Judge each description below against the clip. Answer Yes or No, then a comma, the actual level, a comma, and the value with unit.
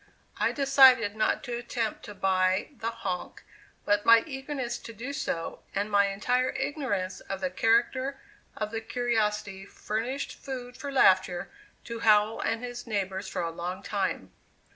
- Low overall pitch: No, high, 225 Hz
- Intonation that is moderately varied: Yes, average, 4.2 semitones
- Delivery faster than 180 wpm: No, average, 155 wpm